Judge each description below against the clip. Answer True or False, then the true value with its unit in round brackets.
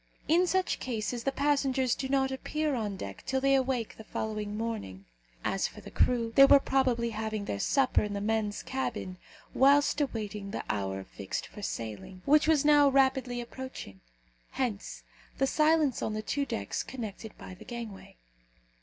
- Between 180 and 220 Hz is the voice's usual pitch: False (240 Hz)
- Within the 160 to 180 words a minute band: True (170 wpm)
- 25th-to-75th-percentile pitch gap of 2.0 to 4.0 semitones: False (4.6 semitones)